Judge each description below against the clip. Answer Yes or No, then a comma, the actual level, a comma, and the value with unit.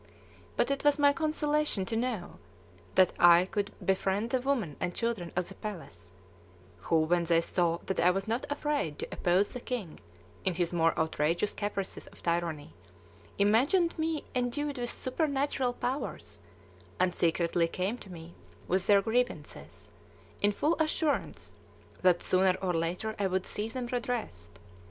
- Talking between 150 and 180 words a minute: Yes, average, 155 wpm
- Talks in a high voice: Yes, high, 200 Hz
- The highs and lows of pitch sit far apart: Yes, wide, 6.3 semitones